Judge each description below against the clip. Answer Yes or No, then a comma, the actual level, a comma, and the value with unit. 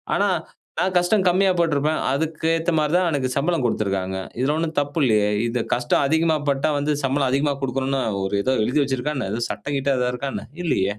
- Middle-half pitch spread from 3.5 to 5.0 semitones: Yes, average, 4.1 semitones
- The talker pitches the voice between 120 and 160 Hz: Yes, medium, 140 Hz